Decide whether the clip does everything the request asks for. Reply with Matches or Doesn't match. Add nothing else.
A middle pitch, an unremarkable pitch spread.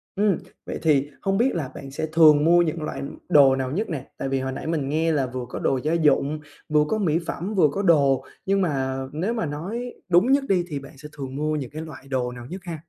Matches